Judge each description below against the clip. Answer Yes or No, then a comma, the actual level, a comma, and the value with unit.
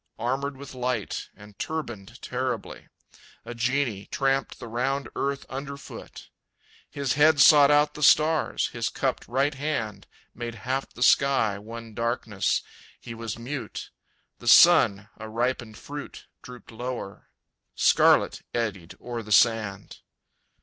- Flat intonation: No, average, 3.7 semitones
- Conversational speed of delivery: No, slow, 130 wpm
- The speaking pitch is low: Yes, low, 125 Hz